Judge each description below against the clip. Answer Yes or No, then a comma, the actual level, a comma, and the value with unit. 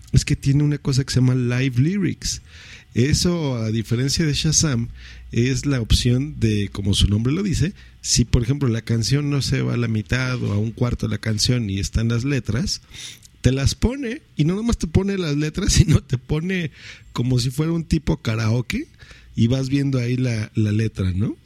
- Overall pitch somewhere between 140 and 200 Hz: No, low, 125 Hz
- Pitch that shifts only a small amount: No, average, 4.4 semitones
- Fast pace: Yes, fast, 205 wpm